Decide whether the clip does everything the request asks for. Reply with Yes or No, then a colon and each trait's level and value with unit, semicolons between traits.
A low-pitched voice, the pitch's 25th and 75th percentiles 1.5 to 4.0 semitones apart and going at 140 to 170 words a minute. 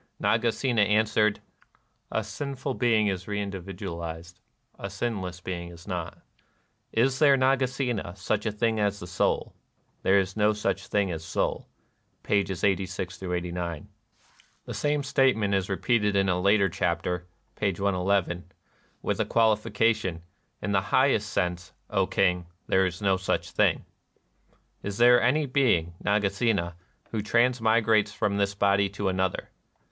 Yes: low, 100 Hz; average, 3.3 semitones; average, 160 wpm